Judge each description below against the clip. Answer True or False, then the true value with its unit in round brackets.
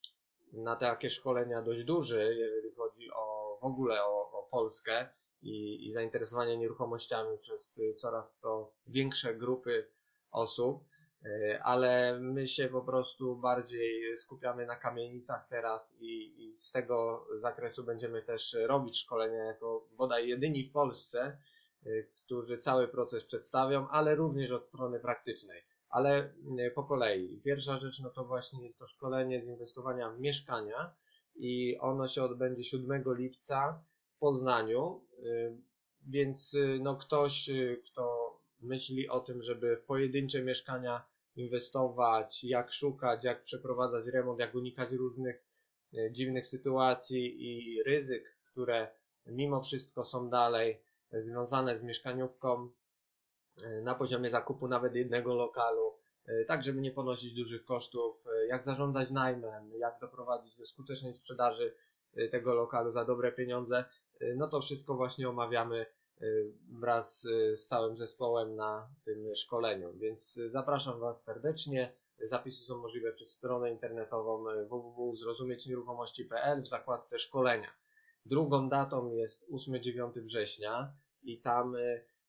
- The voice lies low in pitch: True (125 Hz)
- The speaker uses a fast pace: False (125 wpm)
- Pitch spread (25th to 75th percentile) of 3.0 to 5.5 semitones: False (2.6 semitones)